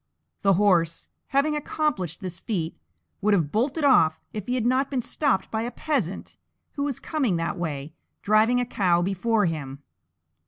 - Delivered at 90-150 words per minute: No, average, 165 wpm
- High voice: Yes, high, 210 Hz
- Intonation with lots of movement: Yes, wide, 6.9 semitones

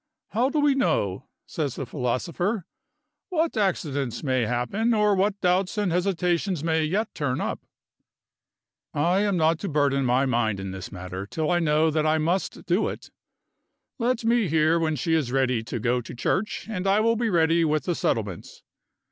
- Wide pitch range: Yes, wide, 6.9 semitones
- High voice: No, medium, 160 Hz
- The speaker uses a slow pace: No, average, 180 wpm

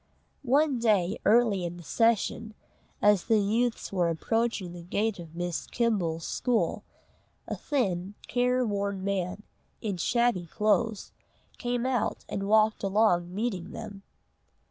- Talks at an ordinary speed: No, slow, 130 wpm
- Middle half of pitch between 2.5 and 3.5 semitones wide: No, average, 4.2 semitones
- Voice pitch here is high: Yes, high, 210 Hz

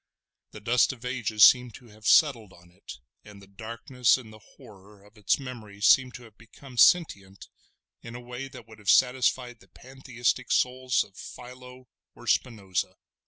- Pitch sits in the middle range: No, low, 115 Hz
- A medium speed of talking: Yes, average, 170 wpm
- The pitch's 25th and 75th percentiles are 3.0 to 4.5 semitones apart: Yes, average, 3.4 semitones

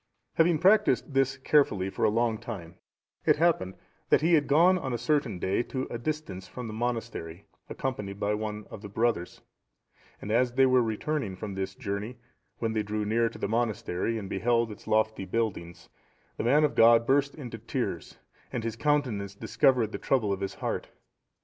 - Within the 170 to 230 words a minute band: Yes, average, 180 wpm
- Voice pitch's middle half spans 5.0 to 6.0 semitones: No, average, 4.3 semitones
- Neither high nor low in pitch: No, low, 115 Hz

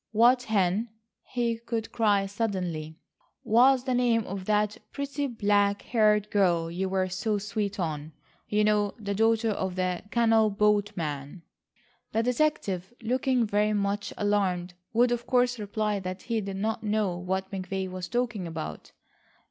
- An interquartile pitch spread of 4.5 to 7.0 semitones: No, average, 3.1 semitones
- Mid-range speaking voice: No, high, 210 Hz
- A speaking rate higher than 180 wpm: No, average, 150 wpm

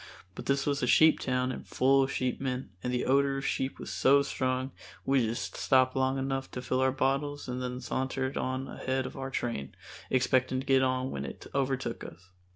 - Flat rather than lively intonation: Yes, narrow, 1.0 semitones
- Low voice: Yes, low, 130 Hz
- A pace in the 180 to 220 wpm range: Yes, fast, 205 wpm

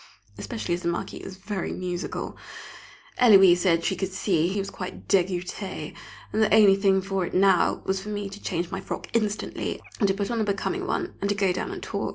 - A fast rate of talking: Yes, fast, 215 wpm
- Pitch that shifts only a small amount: Yes, narrow, 2.2 semitones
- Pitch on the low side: No, high, 195 Hz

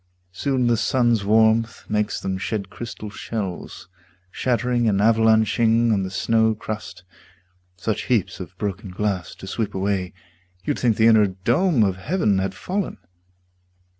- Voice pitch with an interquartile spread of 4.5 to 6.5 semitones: No, average, 3.2 semitones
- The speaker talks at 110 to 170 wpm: Yes, average, 140 wpm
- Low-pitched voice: Yes, low, 110 Hz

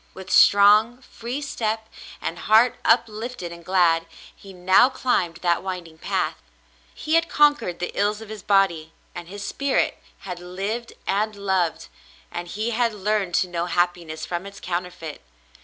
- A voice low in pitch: No, high, 195 Hz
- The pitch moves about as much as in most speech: Yes, average, 3.8 semitones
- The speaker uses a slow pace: No, average, 175 wpm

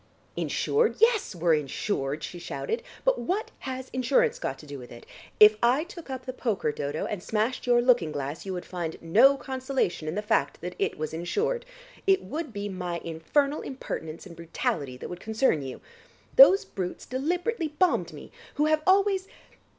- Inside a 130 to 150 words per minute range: No, average, 180 wpm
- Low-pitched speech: No, high, 235 Hz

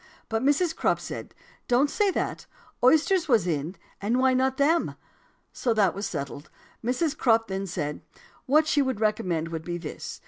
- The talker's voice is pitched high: Yes, high, 230 Hz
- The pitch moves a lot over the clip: Yes, wide, 7.8 semitones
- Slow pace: No, average, 170 wpm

